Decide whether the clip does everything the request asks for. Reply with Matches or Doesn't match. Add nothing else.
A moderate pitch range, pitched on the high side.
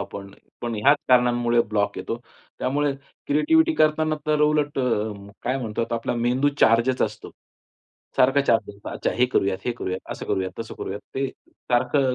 Doesn't match